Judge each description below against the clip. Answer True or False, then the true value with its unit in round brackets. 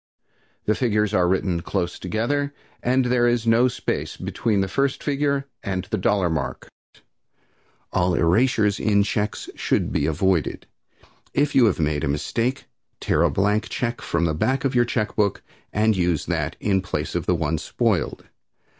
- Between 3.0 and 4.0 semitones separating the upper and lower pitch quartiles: False (5.3 semitones)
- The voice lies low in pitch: True (105 Hz)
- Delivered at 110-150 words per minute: False (165 wpm)